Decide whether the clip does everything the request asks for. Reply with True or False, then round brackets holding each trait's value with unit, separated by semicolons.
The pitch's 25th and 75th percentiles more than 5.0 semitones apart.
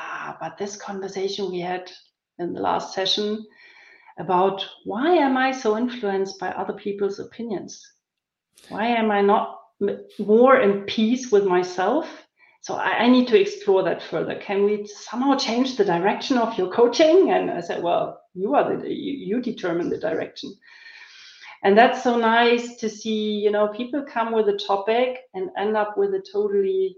True (5.4 semitones)